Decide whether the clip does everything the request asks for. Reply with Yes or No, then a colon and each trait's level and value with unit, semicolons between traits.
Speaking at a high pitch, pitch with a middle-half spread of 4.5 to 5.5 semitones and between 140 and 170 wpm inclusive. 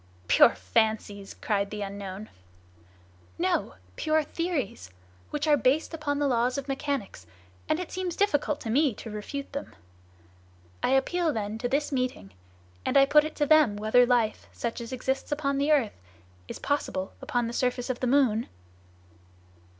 Yes: very high, 255 Hz; average, 5.2 semitones; average, 160 wpm